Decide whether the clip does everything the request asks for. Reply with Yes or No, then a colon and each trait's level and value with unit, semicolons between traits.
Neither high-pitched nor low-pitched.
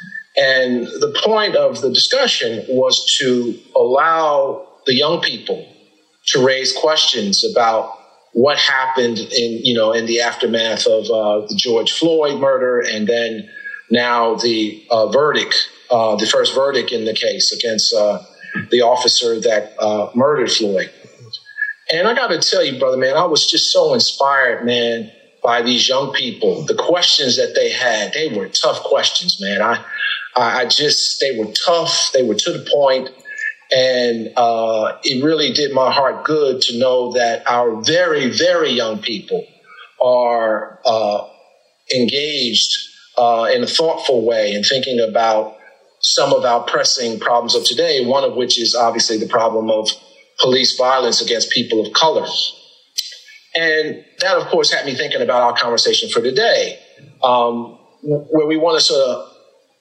Yes: medium, 155 Hz